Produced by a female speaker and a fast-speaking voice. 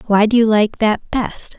Yes: female; fast, 230 wpm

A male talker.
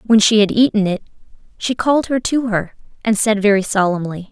No: female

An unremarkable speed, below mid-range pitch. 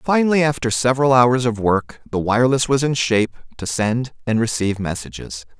Yes: average, 170 wpm; low, 120 Hz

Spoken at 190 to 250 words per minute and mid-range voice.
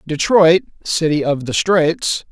No: slow, 130 wpm; medium, 165 Hz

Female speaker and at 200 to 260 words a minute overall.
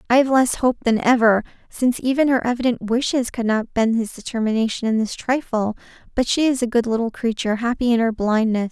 Yes: female; fast, 205 wpm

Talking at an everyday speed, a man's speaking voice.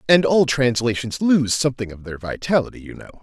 Yes: average, 185 wpm; male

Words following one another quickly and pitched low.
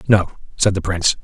No: average, 195 wpm; very low, 95 Hz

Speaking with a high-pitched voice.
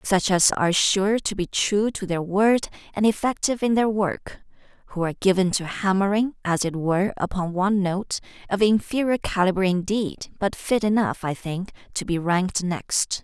Yes: high, 195 Hz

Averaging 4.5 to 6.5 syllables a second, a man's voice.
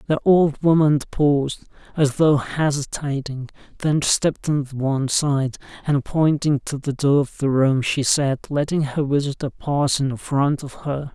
No: 4.3 syllables/s; male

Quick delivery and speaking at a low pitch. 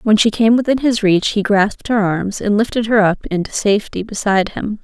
No: fast, 225 wpm; high, 210 Hz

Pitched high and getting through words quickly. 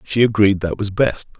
No: low, 105 Hz; fast, 215 wpm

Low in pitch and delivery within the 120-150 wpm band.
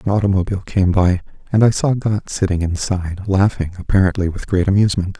No: very low, 95 Hz; average, 175 wpm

